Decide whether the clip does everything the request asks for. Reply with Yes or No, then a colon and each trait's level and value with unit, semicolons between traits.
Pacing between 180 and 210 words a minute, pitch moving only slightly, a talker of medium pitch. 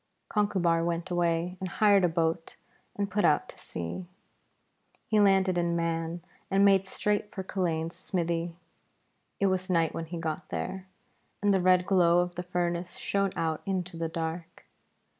No: average, 160 wpm; narrow, 2.3 semitones; medium, 175 Hz